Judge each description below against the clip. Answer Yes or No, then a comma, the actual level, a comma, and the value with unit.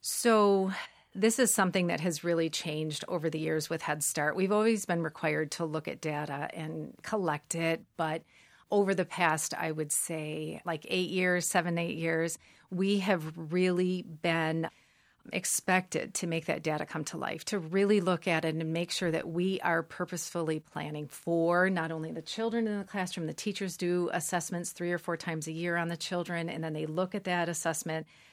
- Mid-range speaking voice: Yes, medium, 170 Hz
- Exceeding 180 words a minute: Yes, average, 195 wpm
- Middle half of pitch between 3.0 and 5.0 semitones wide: No, narrow, 2.5 semitones